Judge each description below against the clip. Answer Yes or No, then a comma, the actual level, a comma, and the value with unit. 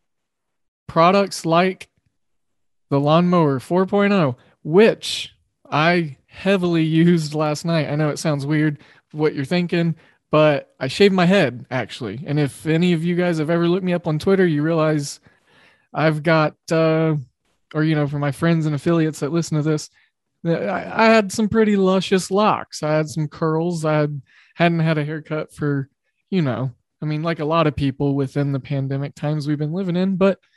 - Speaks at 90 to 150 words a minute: No, average, 175 wpm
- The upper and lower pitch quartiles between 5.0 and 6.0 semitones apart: No, average, 3.0 semitones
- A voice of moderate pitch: Yes, medium, 155 Hz